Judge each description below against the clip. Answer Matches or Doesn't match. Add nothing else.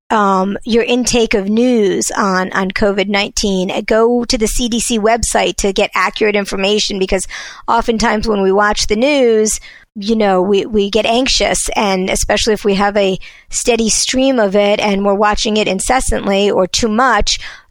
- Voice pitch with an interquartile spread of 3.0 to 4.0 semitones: Doesn't match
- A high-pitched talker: Matches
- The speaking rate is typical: Matches